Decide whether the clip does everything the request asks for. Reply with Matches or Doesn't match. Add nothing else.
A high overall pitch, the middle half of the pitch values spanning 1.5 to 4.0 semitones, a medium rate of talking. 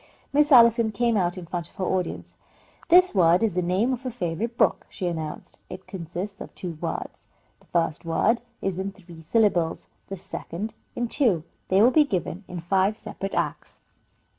Doesn't match